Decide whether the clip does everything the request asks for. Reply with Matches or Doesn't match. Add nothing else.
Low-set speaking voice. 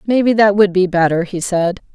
Doesn't match